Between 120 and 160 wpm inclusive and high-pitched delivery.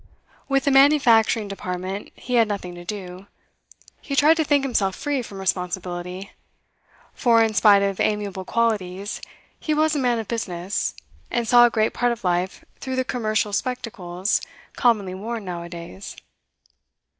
Yes: average, 155 wpm; high, 210 Hz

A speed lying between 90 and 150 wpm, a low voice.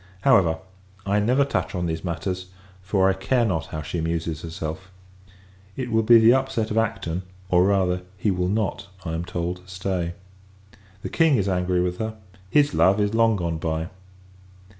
No: average, 175 wpm; very low, 95 Hz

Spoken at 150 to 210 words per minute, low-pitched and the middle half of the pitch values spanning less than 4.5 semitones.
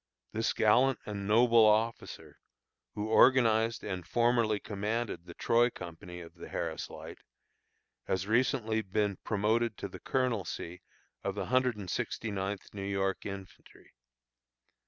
No: slow, 135 wpm; low, 105 Hz; average, 3.0 semitones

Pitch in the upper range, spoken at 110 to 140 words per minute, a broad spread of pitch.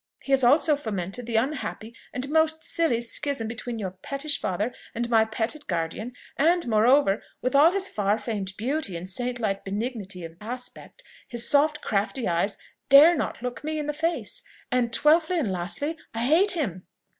No: high, 245 Hz; average, 175 wpm; wide, 6.0 semitones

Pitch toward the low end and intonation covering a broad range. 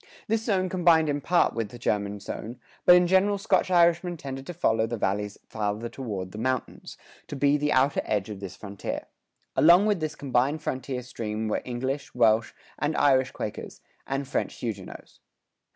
Yes: low, 130 Hz; wide, 6.7 semitones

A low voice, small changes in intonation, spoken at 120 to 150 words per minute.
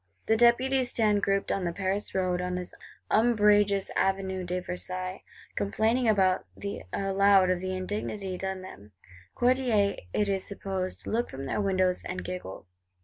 No: high, 195 Hz; narrow, 2.2 semitones; average, 145 wpm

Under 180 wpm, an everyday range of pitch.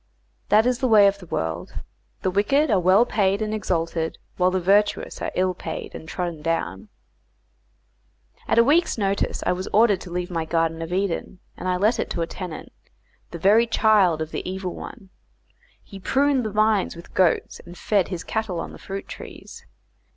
No: average, 190 wpm; average, 3.8 semitones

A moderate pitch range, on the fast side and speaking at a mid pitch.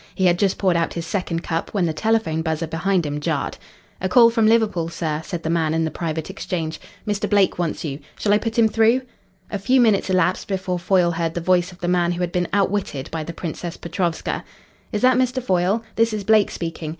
Yes: average, 3.9 semitones; fast, 225 wpm; medium, 180 Hz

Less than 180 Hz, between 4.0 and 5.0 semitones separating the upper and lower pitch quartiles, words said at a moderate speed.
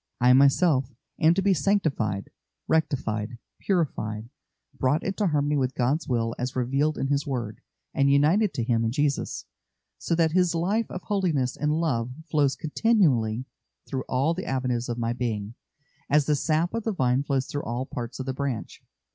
Yes: medium, 140 Hz; average, 4.7 semitones; average, 170 wpm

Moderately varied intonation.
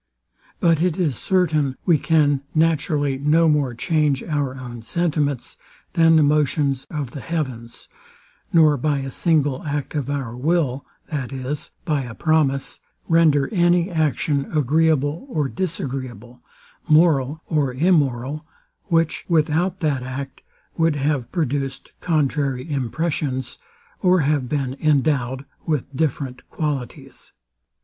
Yes: average, 3.1 semitones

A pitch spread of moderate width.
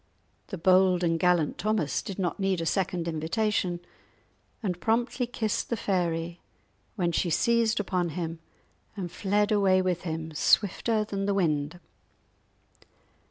Yes: average, 3.5 semitones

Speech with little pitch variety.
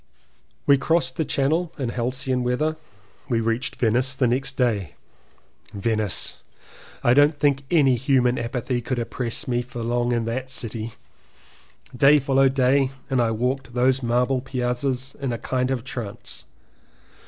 Yes: narrow, 2.1 semitones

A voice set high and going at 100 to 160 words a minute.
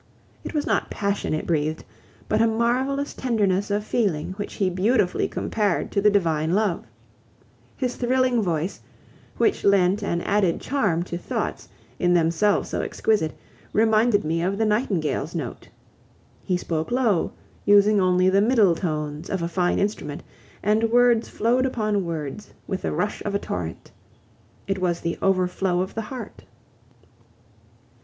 Yes: high, 200 Hz; average, 150 wpm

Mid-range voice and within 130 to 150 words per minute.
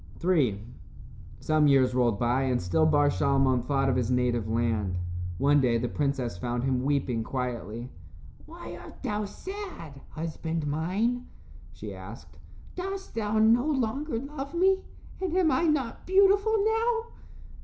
Yes: medium, 145 Hz; average, 145 wpm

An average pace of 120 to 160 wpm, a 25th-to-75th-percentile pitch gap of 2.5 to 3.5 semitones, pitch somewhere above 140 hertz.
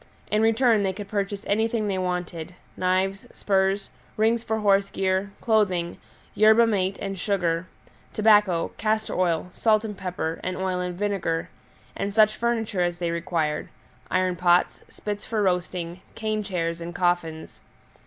Yes: average, 145 wpm; average, 3.1 semitones; high, 190 Hz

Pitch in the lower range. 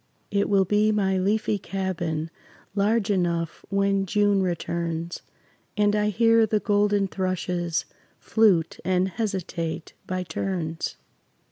No: high, 195 Hz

